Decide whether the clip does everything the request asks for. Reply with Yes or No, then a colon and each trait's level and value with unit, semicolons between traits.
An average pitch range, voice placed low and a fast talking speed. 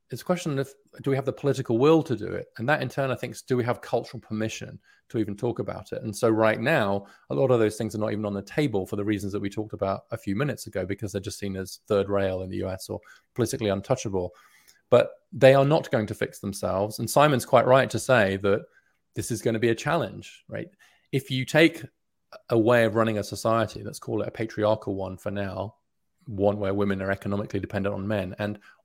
Yes: average, 4.1 semitones; low, 110 Hz; fast, 245 wpm